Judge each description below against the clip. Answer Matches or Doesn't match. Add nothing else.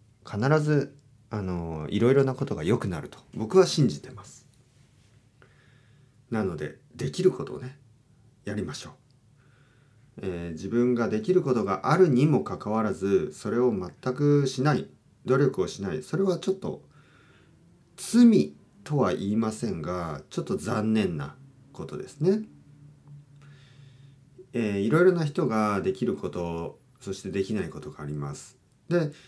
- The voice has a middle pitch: Doesn't match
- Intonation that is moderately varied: Matches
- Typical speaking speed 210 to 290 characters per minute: Matches